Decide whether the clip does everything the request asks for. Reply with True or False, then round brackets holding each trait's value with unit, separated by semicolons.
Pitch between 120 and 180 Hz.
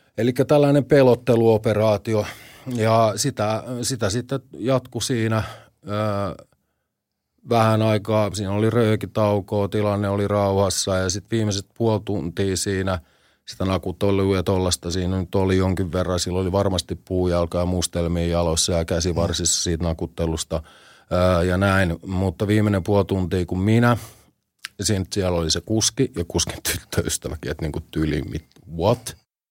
False (100 Hz)